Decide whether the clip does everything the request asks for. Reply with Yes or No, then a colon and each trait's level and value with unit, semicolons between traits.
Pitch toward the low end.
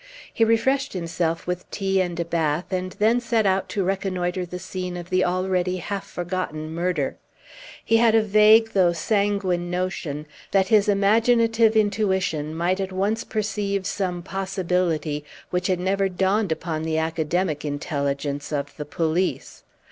No: medium, 185 Hz